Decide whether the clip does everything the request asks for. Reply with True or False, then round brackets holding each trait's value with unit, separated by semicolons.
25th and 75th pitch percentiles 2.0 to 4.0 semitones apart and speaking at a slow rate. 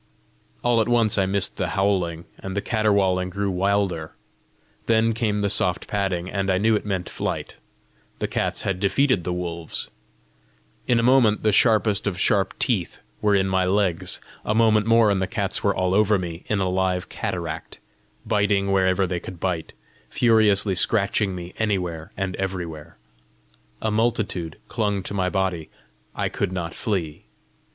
False (2.7 semitones; 165 wpm)